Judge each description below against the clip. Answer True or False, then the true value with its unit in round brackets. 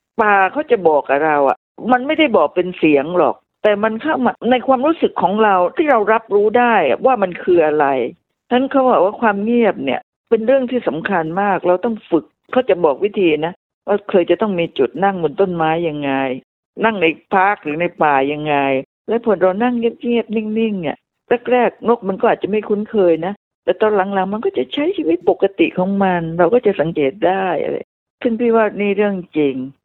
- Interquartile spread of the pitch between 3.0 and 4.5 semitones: False (5.1 semitones)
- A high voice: True (200 Hz)